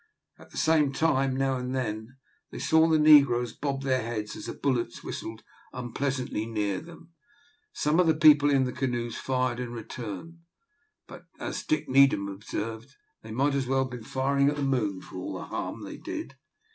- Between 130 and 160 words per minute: No, average, 185 wpm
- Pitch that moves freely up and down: No, average, 3.2 semitones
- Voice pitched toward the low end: Yes, low, 130 Hz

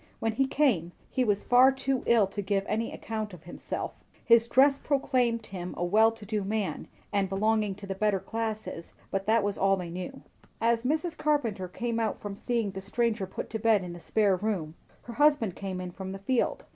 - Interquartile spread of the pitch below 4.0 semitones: Yes, average, 3.3 semitones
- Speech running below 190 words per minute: No, fast, 205 wpm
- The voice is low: No, high, 215 Hz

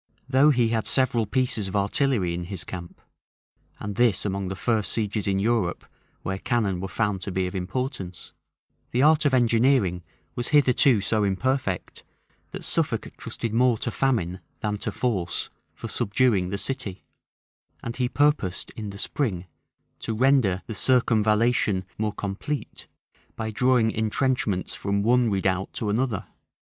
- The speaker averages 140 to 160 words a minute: Yes, average, 155 wpm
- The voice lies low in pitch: Yes, low, 110 Hz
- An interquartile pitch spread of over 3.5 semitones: Yes, average, 4.5 semitones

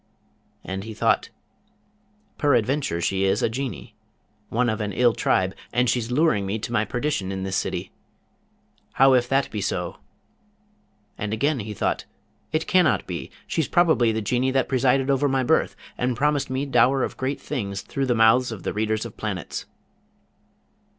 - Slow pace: No, average, 170 wpm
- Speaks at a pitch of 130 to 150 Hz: No, low, 120 Hz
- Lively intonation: No, average, 4.2 semitones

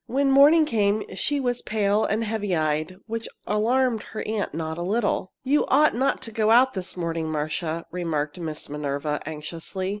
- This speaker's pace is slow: No, average, 170 wpm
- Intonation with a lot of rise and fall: Yes, wide, 6.7 semitones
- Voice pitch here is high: Yes, high, 200 Hz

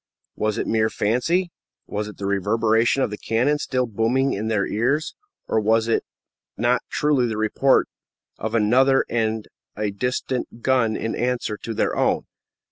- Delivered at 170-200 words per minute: No, average, 160 wpm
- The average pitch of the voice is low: Yes, low, 115 Hz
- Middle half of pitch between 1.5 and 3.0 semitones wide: Yes, average, 2.7 semitones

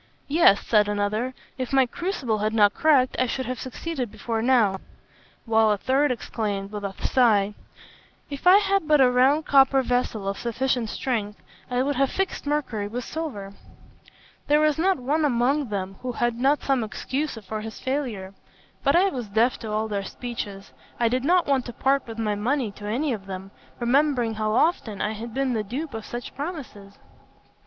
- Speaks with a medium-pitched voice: No, high, 245 Hz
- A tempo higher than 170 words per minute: Yes, average, 190 wpm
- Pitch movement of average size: Yes, average, 4.5 semitones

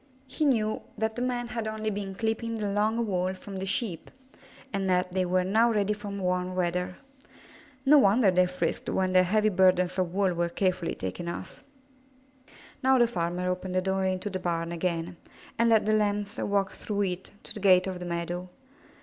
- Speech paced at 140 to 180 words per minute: No, average, 195 wpm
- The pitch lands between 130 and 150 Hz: No, high, 190 Hz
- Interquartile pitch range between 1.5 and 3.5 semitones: Yes, average, 2.9 semitones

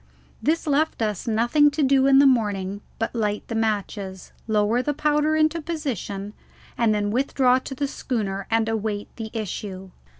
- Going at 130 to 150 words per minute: No, average, 165 wpm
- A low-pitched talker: No, high, 225 Hz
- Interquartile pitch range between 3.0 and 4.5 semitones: No, average, 5.1 semitones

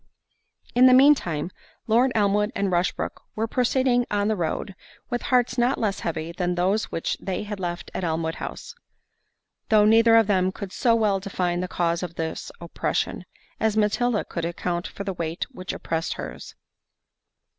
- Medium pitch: No, high, 200 Hz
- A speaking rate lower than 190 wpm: Yes, average, 170 wpm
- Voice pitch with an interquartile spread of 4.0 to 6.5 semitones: Yes, average, 4.5 semitones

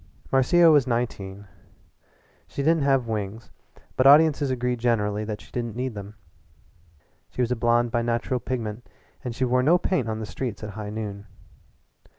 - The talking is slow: No, average, 165 wpm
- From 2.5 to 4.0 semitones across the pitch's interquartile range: Yes, average, 3.3 semitones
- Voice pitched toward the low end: Yes, low, 120 Hz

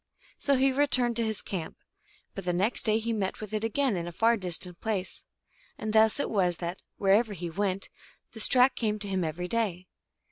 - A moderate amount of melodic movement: Yes, average, 3.9 semitones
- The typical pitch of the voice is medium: No, high, 210 Hz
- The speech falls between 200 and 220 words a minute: Yes, fast, 205 wpm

